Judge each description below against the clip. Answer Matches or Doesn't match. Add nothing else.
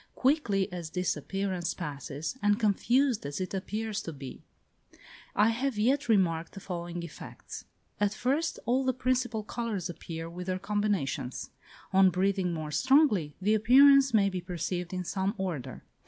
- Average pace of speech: Matches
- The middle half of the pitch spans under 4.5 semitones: Doesn't match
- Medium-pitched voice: Doesn't match